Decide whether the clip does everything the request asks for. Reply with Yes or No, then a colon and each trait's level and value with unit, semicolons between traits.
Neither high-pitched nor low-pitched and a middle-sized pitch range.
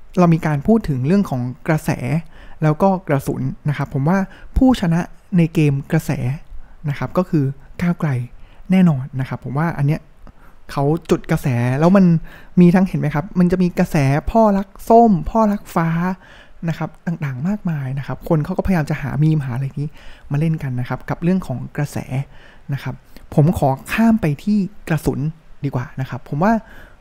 Yes: medium, 155 Hz; average, 4.6 semitones